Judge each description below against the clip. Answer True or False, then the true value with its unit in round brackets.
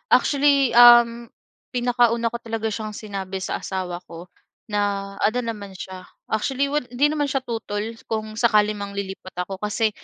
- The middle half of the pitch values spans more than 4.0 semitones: False (3.3 semitones)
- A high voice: True (220 Hz)